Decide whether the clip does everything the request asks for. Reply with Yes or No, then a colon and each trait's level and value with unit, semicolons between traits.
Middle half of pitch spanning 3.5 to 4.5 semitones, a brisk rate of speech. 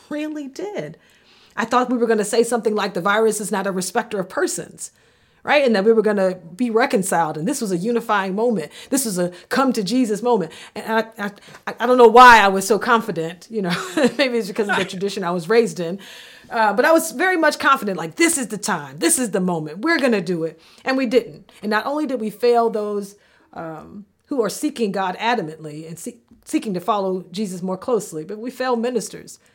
Yes: average, 4.2 semitones; fast, 230 wpm